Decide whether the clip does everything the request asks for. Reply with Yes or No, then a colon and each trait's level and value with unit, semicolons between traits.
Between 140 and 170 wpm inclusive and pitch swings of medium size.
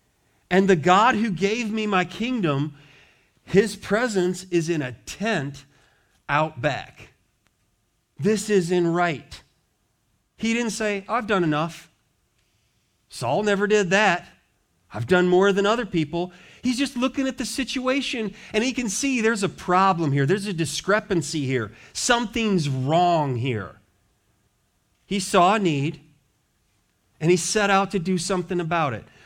No: average, 145 wpm; wide, 7.9 semitones